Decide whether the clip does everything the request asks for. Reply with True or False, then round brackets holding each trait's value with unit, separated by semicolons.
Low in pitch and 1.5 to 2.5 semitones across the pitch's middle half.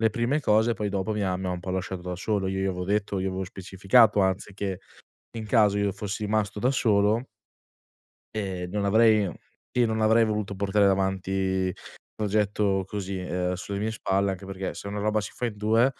True (100 Hz; 2.1 semitones)